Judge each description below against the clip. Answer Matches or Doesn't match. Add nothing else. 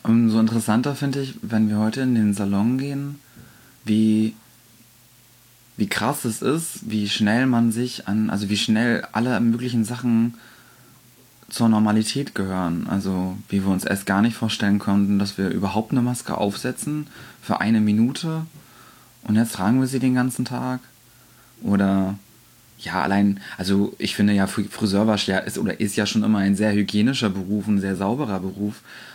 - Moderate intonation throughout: Matches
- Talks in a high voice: Doesn't match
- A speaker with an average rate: Matches